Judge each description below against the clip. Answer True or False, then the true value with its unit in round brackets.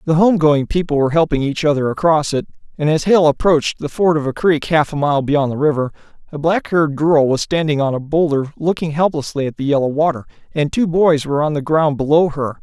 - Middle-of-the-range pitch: True (150 Hz)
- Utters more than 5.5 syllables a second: True (5.8 syllables/s)